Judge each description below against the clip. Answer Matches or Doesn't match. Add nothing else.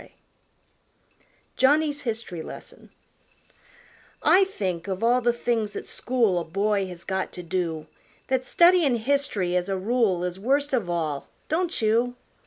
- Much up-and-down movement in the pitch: Matches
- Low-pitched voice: Doesn't match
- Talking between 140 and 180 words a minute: Matches